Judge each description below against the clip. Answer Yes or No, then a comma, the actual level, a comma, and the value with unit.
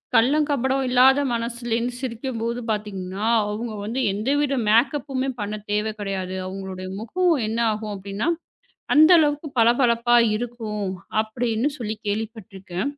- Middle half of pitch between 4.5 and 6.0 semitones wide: No, average, 3.7 semitones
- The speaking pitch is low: No, high, 230 Hz